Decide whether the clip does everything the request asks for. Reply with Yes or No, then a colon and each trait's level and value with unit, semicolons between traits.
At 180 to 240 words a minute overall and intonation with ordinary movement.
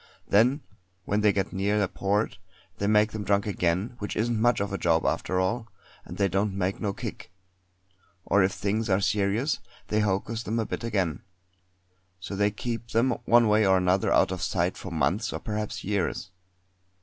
No: average, 185 wpm; narrow, 2.3 semitones